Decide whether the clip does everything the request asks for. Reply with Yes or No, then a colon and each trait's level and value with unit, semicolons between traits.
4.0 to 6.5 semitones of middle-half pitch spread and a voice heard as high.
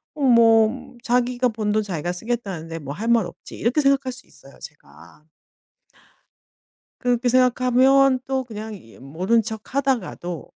Yes: average, 5.2 semitones; high, 230 Hz